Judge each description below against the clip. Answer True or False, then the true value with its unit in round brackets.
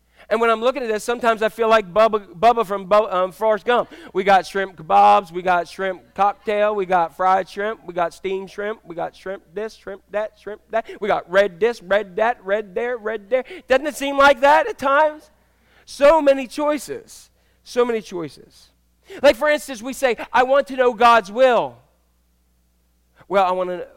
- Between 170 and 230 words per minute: True (200 wpm)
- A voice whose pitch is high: True (220 Hz)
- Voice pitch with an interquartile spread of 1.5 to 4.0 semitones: False (5.3 semitones)